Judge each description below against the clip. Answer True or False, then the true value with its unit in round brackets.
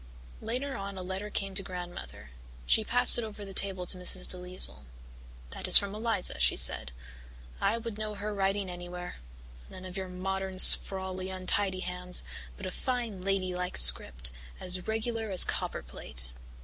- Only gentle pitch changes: True (2.2 semitones)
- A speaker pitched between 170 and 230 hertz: True (190 Hz)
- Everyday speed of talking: True (160 wpm)